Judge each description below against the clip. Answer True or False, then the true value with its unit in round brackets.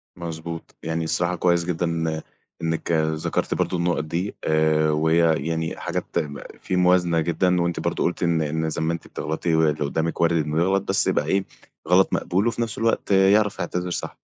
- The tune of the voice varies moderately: False (1.9 semitones)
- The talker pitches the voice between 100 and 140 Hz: False (85 Hz)